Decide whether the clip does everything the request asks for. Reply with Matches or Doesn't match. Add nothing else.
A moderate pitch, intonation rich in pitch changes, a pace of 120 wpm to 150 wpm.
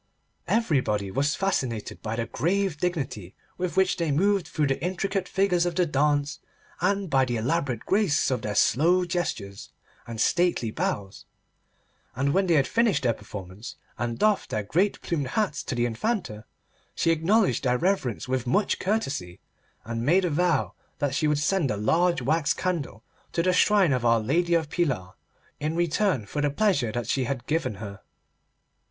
Doesn't match